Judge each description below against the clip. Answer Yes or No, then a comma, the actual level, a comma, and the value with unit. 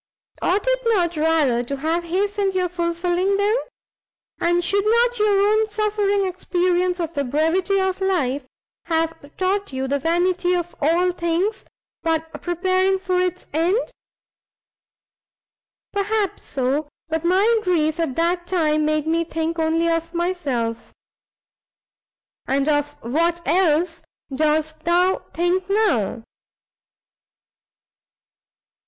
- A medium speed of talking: No, slow, 120 wpm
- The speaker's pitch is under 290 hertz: No, very high, 345 Hz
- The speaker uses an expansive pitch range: No, average, 3.1 semitones